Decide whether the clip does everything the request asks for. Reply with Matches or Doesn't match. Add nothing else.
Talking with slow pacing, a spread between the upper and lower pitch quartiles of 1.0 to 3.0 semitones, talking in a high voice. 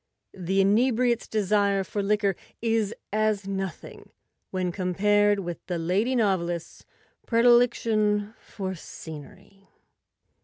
Matches